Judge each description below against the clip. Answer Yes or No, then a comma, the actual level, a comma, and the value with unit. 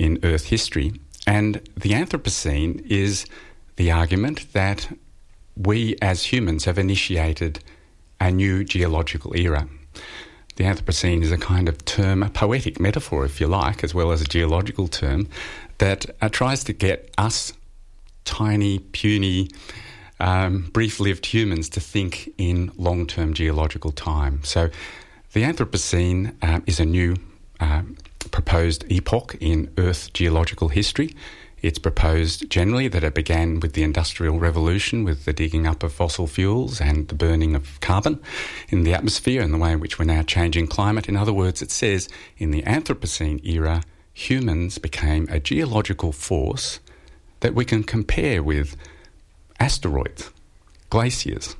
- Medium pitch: No, very low, 85 Hz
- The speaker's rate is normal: Yes, average, 145 wpm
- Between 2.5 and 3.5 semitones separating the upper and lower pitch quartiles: No, average, 4.0 semitones